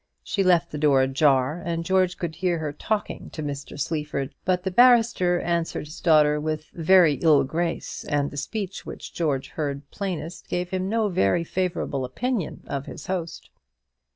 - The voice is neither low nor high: Yes, medium, 165 Hz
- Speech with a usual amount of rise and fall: Yes, average, 3.8 semitones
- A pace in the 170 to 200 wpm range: Yes, average, 175 wpm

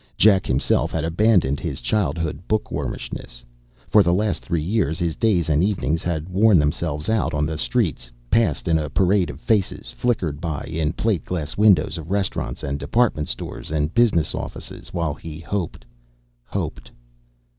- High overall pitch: No, very low, 85 Hz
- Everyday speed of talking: Yes, average, 160 wpm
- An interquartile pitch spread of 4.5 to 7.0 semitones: Yes, average, 4.9 semitones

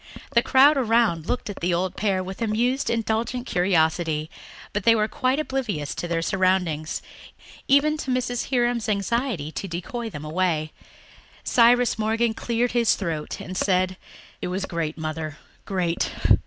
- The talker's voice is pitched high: Yes, high, 200 Hz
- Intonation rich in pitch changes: Yes, wide, 5.9 semitones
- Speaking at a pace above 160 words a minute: No, average, 150 wpm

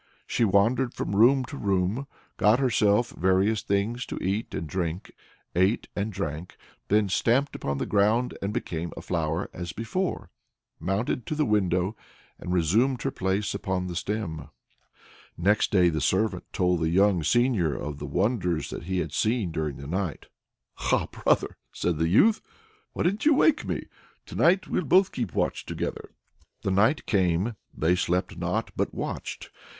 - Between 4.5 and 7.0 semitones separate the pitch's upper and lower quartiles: Yes, average, 4.8 semitones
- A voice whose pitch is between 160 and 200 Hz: No, low, 100 Hz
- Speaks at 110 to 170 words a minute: Yes, average, 165 wpm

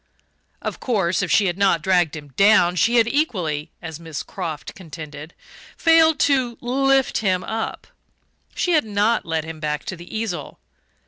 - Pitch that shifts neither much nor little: No, wide, 6.4 semitones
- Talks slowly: No, average, 165 wpm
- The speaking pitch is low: No, medium, 185 Hz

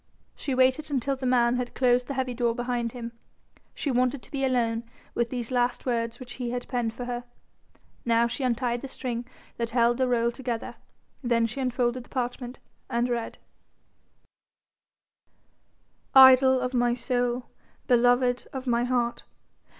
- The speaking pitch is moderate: No, high, 245 Hz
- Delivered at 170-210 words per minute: No, average, 160 wpm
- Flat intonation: Yes, narrow, 1.3 semitones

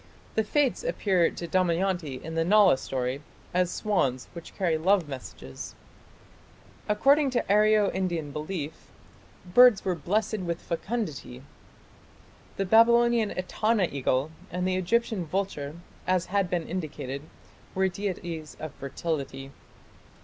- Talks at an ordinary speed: No, slow, 120 wpm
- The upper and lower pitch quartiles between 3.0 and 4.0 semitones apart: No, average, 4.9 semitones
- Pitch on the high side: No, medium, 180 Hz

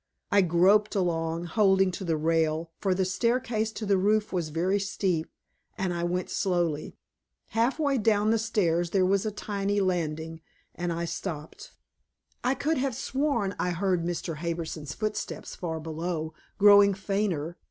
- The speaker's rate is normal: Yes, average, 155 wpm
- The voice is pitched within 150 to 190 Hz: Yes, medium, 185 Hz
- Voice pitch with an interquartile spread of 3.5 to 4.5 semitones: Yes, average, 3.8 semitones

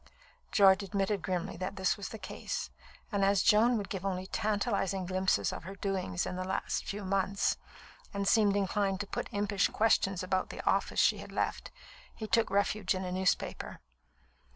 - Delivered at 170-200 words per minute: Yes, average, 175 wpm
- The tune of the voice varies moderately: No, narrow, 1.4 semitones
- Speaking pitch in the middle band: No, high, 195 Hz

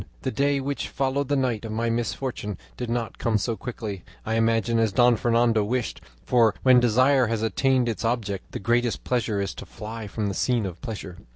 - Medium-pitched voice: No, low, 115 Hz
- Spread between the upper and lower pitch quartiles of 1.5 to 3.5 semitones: Yes, narrow, 2.4 semitones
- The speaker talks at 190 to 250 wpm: Yes, average, 200 wpm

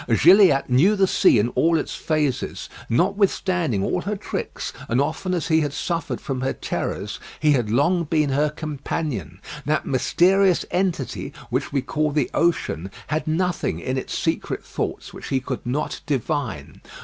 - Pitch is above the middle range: No, medium, 150 Hz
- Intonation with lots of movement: No, average, 5.0 semitones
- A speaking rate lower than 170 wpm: Yes, average, 160 wpm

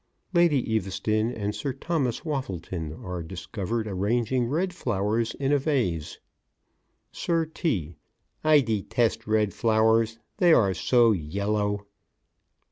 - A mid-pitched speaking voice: No, low, 110 Hz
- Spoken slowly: Yes, slow, 120 wpm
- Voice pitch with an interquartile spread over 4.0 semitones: Yes, average, 5.1 semitones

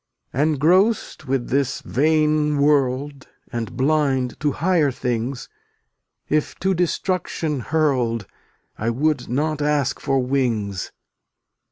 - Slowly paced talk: Yes, slow, 115 wpm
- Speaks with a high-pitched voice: No, medium, 140 Hz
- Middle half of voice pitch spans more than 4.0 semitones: No, average, 3.4 semitones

